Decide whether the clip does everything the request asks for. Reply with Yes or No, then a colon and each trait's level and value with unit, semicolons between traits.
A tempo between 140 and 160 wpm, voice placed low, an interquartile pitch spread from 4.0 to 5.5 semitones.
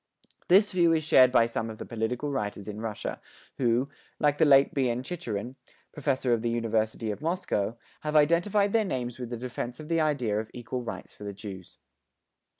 No: average, 190 wpm; low, 125 Hz; average, 5.2 semitones